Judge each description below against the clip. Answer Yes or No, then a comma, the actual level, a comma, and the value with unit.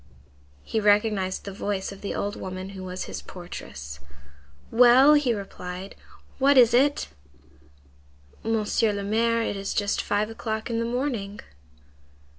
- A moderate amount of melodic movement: Yes, average, 3.0 semitones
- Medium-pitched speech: No, high, 210 Hz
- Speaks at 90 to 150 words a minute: Yes, average, 140 wpm